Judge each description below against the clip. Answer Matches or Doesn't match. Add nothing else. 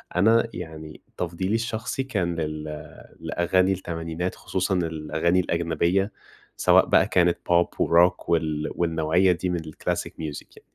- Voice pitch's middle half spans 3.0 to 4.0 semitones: Doesn't match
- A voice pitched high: Doesn't match